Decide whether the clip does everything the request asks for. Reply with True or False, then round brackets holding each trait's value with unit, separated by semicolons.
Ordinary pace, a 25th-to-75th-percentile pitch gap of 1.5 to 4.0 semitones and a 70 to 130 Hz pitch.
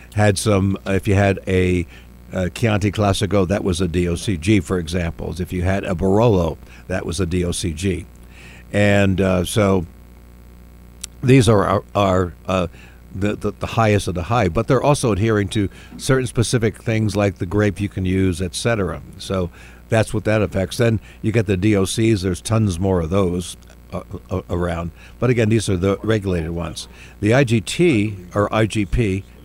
True (170 wpm; 3.1 semitones; 95 Hz)